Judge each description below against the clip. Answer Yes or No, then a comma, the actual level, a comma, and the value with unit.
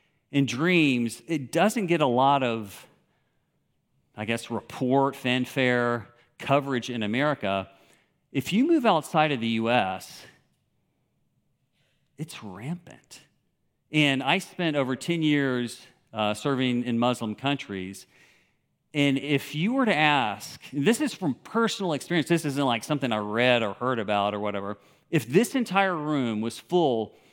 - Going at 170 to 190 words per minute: No, average, 140 wpm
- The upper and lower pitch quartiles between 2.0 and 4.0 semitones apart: No, average, 4.7 semitones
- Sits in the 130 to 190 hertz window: Yes, low, 135 Hz